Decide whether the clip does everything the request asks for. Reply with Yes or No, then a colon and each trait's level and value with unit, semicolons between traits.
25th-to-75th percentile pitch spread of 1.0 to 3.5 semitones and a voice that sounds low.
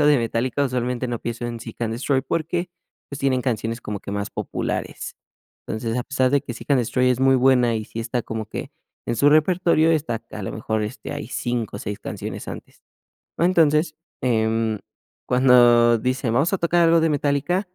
No: average, 4.1 semitones; low, 125 Hz